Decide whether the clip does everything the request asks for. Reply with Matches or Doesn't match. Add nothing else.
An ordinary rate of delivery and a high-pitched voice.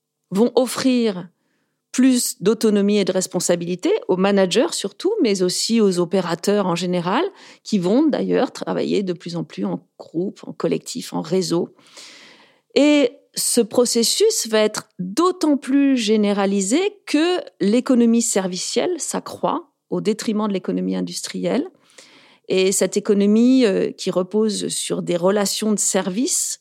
Doesn't match